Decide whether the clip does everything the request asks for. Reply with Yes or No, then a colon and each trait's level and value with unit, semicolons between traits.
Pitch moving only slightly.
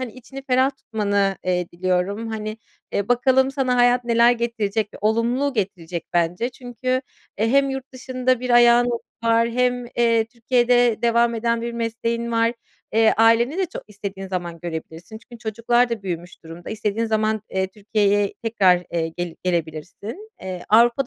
No: average, 3.6 semitones